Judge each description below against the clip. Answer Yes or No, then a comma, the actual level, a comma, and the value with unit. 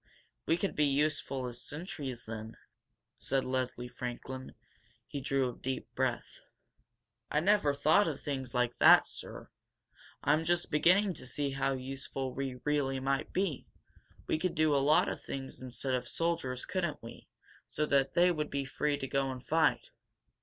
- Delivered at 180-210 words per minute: No, average, 165 wpm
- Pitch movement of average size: Yes, average, 3.0 semitones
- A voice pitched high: No, low, 135 Hz